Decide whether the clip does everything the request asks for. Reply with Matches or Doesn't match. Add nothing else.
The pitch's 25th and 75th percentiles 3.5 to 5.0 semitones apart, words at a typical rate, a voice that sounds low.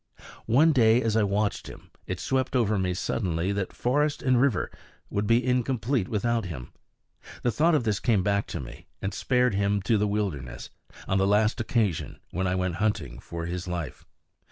Matches